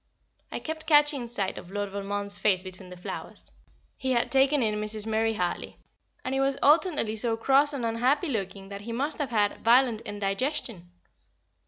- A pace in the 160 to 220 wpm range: Yes, average, 175 wpm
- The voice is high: Yes, high, 230 Hz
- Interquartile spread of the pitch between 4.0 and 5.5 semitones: Yes, average, 5.0 semitones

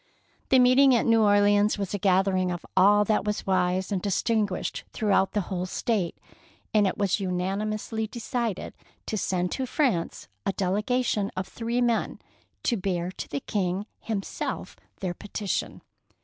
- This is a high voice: Yes, high, 205 Hz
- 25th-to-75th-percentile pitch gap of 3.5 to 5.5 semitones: No, average, 2.9 semitones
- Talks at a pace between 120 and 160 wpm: Yes, average, 155 wpm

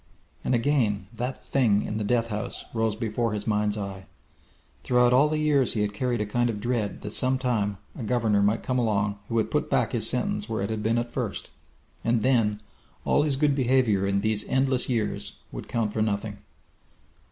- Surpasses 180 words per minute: Yes, average, 195 wpm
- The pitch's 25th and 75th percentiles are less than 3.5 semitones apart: Yes, average, 3.1 semitones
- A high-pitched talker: No, low, 110 Hz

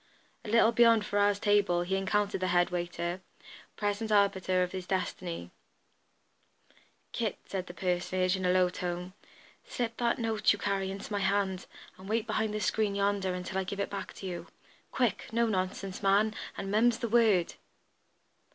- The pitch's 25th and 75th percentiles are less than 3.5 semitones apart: Yes, narrow, 2.5 semitones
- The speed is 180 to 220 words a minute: No, average, 170 wpm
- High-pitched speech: Yes, high, 195 Hz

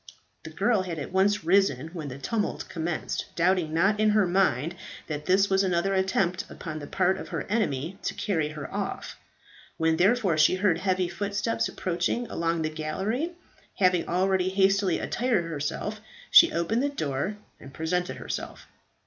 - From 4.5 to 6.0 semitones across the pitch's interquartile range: No, average, 3.6 semitones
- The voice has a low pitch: No, medium, 185 Hz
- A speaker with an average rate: Yes, average, 165 wpm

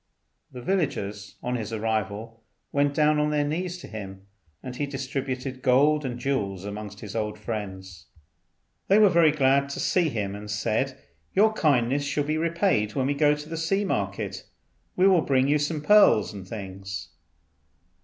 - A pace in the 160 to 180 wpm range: Yes, average, 170 wpm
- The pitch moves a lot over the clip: Yes, wide, 6.1 semitones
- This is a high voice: No, low, 130 Hz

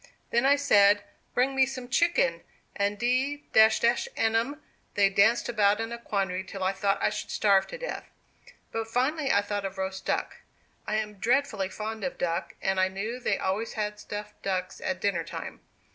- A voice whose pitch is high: Yes, high, 215 Hz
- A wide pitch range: No, average, 3.9 semitones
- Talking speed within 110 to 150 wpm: No, average, 185 wpm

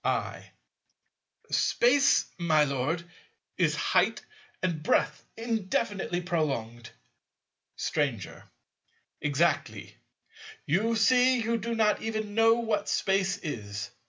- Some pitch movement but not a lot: No, wide, 7.3 semitones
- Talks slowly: Yes, slow, 95 wpm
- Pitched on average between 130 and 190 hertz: Yes, medium, 185 Hz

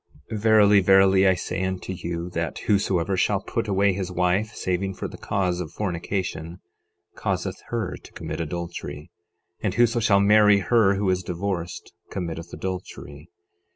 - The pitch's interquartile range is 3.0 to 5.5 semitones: No, narrow, 2.4 semitones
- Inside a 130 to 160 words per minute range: Yes, average, 155 wpm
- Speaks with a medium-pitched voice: No, very low, 95 Hz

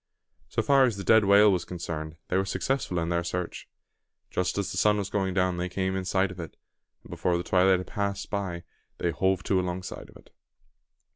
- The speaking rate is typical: No, fast, 215 wpm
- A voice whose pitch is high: No, very low, 95 Hz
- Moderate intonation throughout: No, narrow, 2.1 semitones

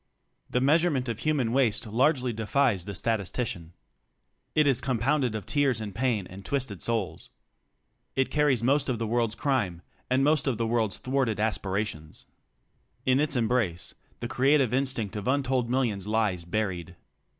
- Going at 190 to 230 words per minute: No, average, 155 wpm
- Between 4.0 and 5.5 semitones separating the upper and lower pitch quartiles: Yes, average, 4.3 semitones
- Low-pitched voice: Yes, low, 120 Hz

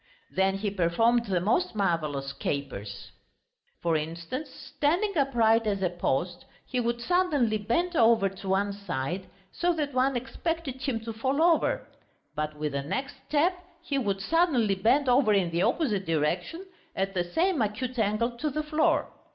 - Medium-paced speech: Yes, average, 160 wpm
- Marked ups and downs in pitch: Yes, wide, 7.5 semitones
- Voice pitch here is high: Yes, high, 225 Hz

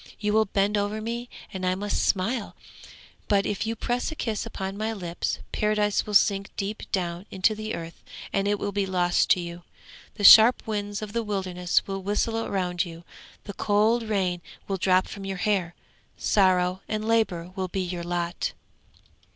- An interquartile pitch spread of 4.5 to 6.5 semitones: No, narrow, 2.6 semitones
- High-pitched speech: Yes, high, 200 Hz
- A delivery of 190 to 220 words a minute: No, average, 180 wpm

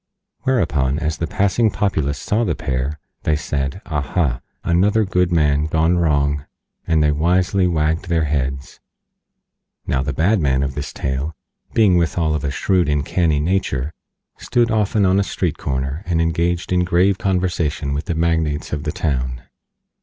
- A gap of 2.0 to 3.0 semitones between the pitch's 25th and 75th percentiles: No, average, 4.0 semitones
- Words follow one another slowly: No, average, 160 wpm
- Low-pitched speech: Yes, very low, 80 Hz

